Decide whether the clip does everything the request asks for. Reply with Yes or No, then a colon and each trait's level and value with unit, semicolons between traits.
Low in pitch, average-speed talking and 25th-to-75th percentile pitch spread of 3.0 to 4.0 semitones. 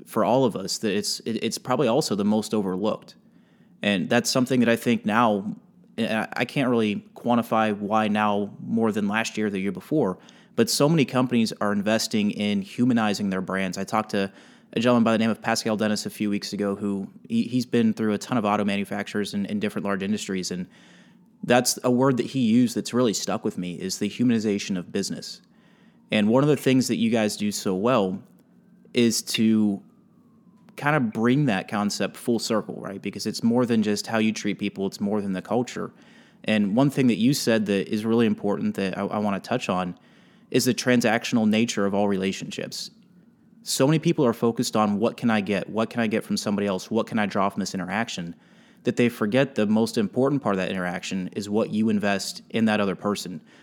No: low, 110 Hz; fast, 215 wpm; average, 3.4 semitones